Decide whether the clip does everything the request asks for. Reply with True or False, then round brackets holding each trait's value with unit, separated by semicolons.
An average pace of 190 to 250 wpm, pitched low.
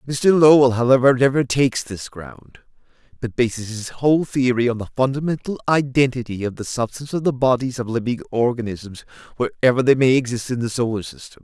False (175 wpm; 125 Hz)